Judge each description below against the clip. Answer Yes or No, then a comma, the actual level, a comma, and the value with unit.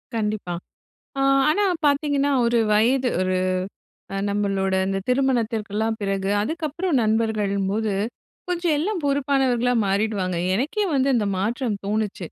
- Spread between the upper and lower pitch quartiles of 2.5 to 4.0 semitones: No, average, 5.3 semitones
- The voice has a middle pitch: No, high, 225 Hz